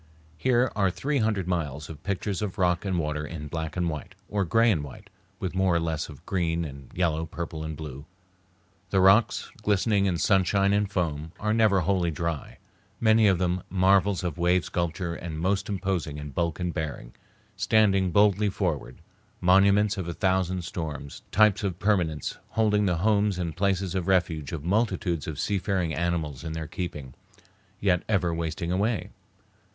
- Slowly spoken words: No, average, 170 wpm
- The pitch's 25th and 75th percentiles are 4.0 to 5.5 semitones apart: No, average, 3.5 semitones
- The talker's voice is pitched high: No, very low, 90 Hz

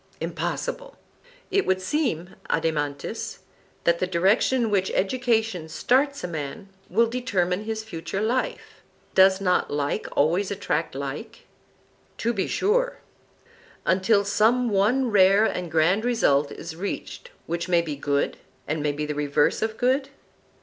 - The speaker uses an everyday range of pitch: No, wide, 6.0 semitones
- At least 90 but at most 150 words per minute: Yes, average, 140 wpm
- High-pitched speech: Yes, high, 195 Hz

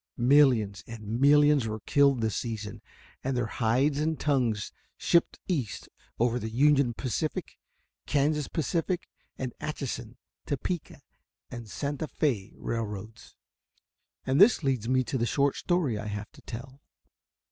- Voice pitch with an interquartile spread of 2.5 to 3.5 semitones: No, average, 4.4 semitones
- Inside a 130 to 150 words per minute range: Yes, slow, 135 wpm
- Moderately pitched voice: No, low, 130 Hz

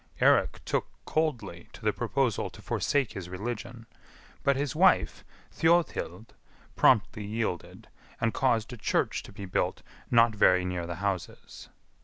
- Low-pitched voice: Yes, low, 110 Hz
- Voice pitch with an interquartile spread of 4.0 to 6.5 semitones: Yes, average, 5.0 semitones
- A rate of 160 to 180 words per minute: No, average, 140 wpm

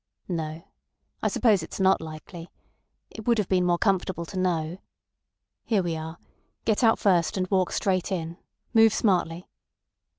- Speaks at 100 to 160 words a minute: Yes, average, 155 wpm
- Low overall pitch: No, medium, 185 Hz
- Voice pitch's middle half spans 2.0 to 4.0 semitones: Yes, average, 3.2 semitones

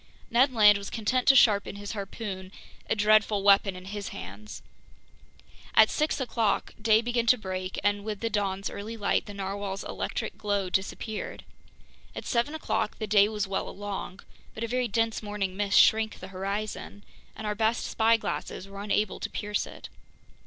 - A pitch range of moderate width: No, narrow, 2.0 semitones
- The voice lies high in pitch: Yes, high, 210 Hz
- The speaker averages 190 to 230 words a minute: No, average, 170 wpm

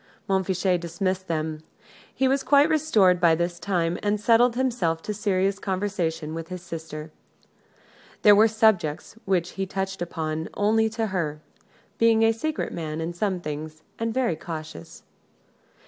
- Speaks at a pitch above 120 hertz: Yes, medium, 185 Hz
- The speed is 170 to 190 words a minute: No, average, 150 wpm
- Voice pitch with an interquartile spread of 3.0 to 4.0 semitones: No, average, 4.9 semitones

